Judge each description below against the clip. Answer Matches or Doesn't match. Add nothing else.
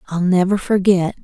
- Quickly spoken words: Doesn't match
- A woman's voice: Matches